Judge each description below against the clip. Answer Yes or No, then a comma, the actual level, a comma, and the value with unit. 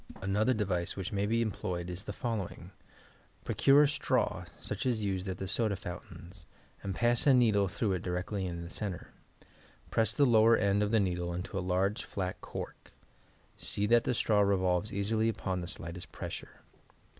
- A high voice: No, low, 100 Hz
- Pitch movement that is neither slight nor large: Yes, average, 3.4 semitones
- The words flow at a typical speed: Yes, average, 180 wpm